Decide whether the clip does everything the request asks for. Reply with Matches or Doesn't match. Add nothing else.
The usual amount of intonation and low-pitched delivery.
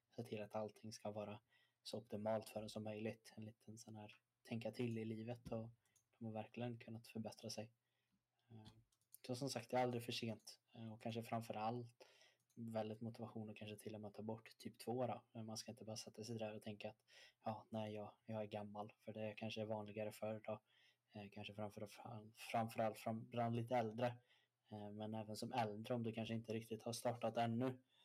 Doesn't match